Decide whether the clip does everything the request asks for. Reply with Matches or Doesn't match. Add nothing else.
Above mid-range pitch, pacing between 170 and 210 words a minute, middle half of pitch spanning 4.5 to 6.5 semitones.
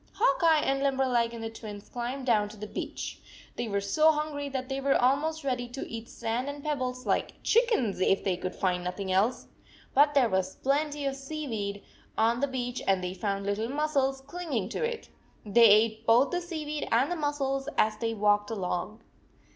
Matches